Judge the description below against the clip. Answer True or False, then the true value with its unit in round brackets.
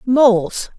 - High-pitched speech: True (230 Hz)